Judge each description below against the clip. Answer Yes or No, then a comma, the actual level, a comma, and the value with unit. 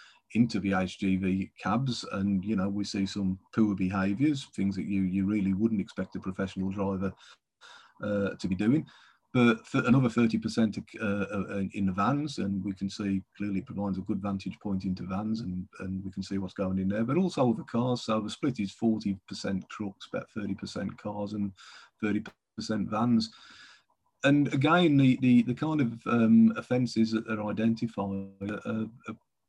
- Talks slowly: No, average, 185 wpm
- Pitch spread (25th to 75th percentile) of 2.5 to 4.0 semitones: Yes, average, 3.0 semitones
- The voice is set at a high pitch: No, low, 100 Hz